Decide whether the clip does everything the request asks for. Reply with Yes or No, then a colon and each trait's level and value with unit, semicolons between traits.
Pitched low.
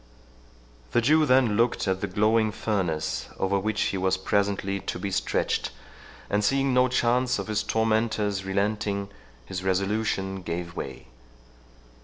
Yes: low, 105 Hz